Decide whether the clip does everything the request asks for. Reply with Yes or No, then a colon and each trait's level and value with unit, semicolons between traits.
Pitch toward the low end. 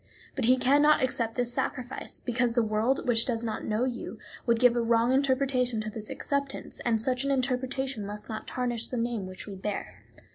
No: high, 245 Hz